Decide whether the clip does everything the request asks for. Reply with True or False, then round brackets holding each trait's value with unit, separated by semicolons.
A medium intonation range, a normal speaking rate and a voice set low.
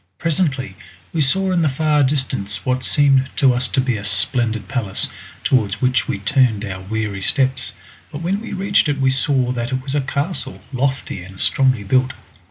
True (4.3 semitones; 185 wpm; 130 Hz)